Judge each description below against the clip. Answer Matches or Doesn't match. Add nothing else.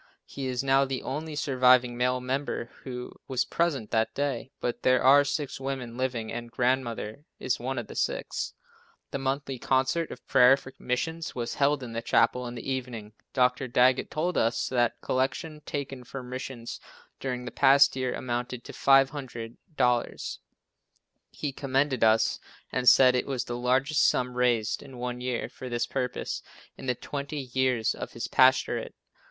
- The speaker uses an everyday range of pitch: Doesn't match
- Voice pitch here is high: Doesn't match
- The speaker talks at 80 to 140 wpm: Doesn't match